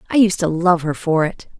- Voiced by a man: No, female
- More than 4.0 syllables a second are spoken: Yes, 5.3 syllables/s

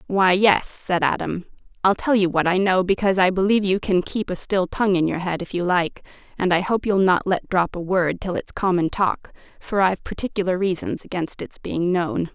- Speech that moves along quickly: Yes, fast, 225 wpm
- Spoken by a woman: Yes, female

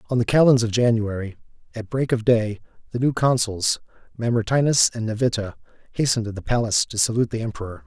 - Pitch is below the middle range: Yes, low, 115 Hz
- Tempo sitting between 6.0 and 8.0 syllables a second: Yes, 6.3 syllables/s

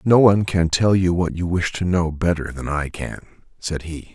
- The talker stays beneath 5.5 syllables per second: Yes, 4.9 syllables/s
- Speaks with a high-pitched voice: No, very low, 85 Hz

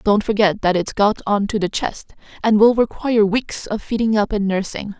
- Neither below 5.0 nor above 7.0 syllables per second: Yes, 5.1 syllables/s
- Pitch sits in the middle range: No, high, 210 Hz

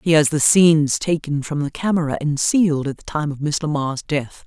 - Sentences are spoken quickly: Yes, fast, 230 wpm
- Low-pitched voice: No, medium, 150 Hz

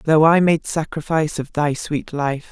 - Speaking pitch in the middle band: Yes, medium, 155 Hz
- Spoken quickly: No, average, 190 wpm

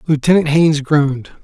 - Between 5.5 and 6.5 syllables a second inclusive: Yes, 5.9 syllables/s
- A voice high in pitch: No, medium, 150 Hz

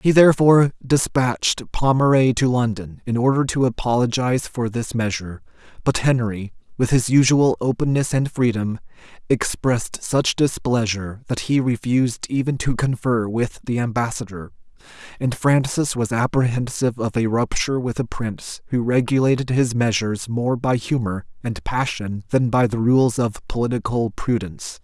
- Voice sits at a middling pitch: No, low, 120 Hz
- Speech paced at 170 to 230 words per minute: No, average, 145 wpm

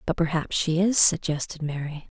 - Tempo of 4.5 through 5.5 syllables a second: Yes, 5.0 syllables/s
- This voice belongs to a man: No, female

